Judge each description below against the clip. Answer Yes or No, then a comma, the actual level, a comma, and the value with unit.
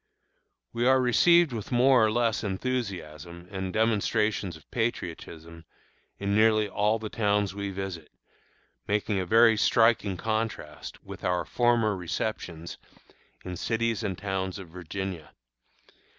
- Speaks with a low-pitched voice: Yes, low, 105 Hz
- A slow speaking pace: Yes, slow, 125 wpm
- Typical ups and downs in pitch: Yes, average, 3.7 semitones